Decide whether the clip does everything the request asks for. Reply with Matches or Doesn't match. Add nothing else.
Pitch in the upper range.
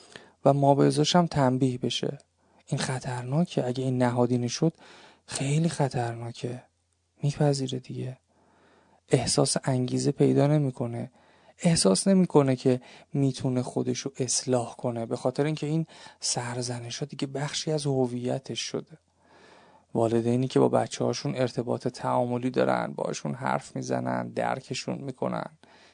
Doesn't match